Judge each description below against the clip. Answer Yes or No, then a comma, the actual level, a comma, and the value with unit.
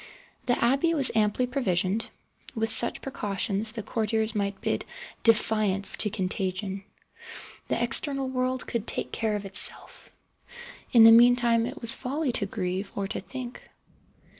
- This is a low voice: No, high, 225 Hz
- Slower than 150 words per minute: Yes, average, 140 wpm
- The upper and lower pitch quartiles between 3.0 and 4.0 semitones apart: Yes, average, 3.7 semitones